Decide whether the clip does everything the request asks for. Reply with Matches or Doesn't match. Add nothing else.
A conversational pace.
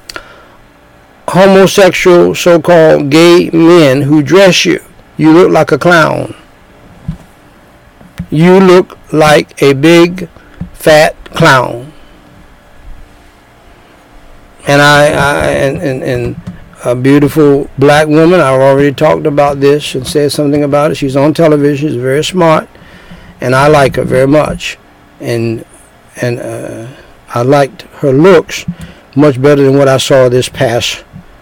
Doesn't match